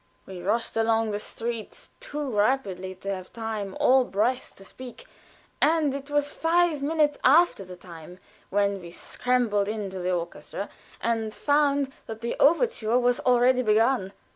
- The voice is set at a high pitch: Yes, high, 230 Hz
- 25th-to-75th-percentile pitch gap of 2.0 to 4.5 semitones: No, wide, 5.5 semitones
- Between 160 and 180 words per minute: No, average, 150 wpm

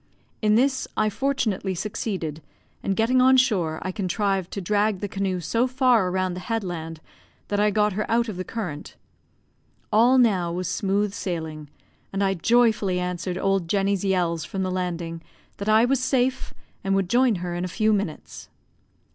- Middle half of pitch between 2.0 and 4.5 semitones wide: Yes, average, 3.6 semitones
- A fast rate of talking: No, average, 170 wpm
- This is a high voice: Yes, high, 195 Hz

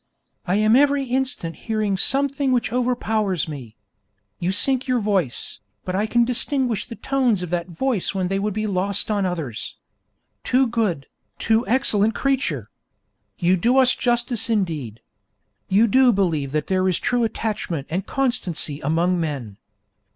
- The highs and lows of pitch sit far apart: Yes, wide, 5.8 semitones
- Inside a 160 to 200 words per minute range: No, average, 150 wpm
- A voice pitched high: Yes, high, 210 Hz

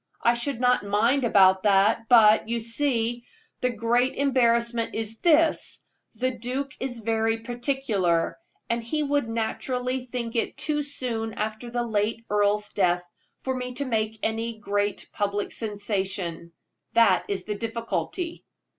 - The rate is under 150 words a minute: Yes, average, 140 wpm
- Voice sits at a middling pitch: No, high, 230 Hz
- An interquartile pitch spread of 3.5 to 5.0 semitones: No, average, 3.1 semitones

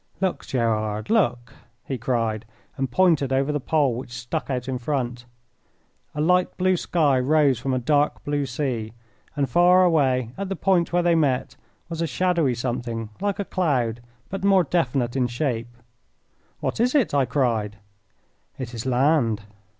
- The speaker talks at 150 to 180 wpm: Yes, average, 165 wpm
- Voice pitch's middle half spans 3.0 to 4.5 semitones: No, wide, 5.4 semitones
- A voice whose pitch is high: No, low, 135 Hz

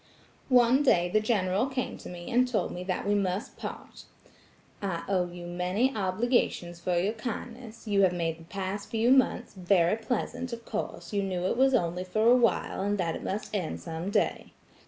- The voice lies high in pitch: Yes, high, 200 Hz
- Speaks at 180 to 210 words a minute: Yes, average, 190 wpm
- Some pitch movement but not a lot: Yes, average, 4.6 semitones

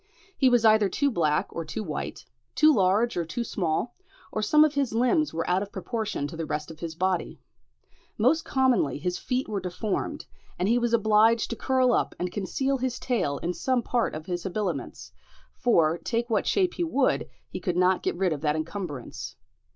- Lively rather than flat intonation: Yes, wide, 6.2 semitones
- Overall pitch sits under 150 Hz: No, high, 210 Hz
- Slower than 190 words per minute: No, average, 195 wpm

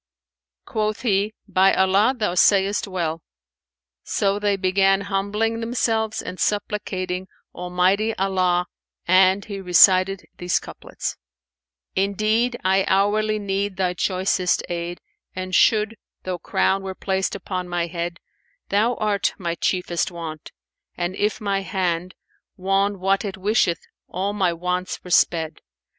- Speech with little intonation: Yes, narrow, 2.2 semitones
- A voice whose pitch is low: No, high, 190 Hz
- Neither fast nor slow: No, slow, 130 wpm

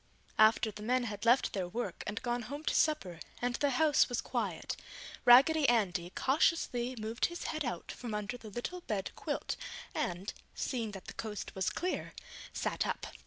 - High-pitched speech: Yes, high, 240 Hz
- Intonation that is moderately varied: Yes, average, 4.2 semitones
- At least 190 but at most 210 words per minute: No, average, 175 wpm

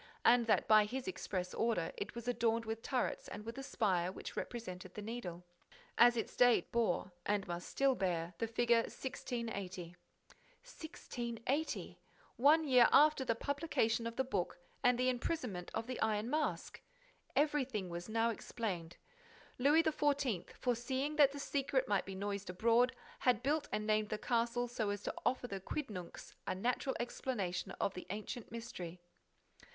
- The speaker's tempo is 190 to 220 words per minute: No, average, 160 wpm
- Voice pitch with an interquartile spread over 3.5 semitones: Yes, average, 4.1 semitones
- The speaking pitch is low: No, high, 230 Hz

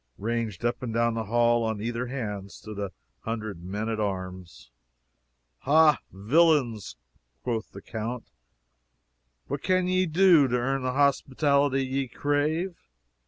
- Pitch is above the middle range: No, low, 120 Hz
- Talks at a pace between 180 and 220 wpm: No, average, 140 wpm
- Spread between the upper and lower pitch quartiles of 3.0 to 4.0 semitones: No, average, 4.7 semitones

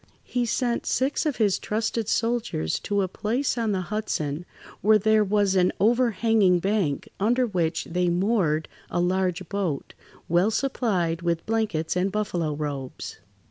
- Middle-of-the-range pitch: No, high, 195 Hz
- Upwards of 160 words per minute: No, average, 145 wpm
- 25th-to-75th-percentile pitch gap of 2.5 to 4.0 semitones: No, average, 4.4 semitones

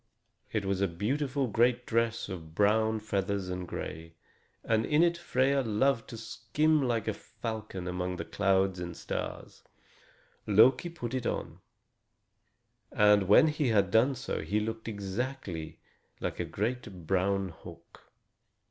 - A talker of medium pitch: No, low, 110 Hz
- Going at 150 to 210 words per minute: No, average, 140 wpm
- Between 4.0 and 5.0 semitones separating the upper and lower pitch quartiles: Yes, average, 4.4 semitones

